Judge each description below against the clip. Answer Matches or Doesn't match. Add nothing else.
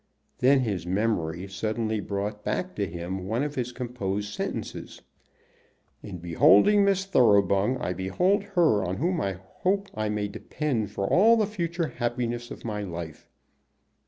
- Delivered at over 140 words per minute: Matches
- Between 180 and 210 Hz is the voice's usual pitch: Doesn't match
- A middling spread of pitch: Doesn't match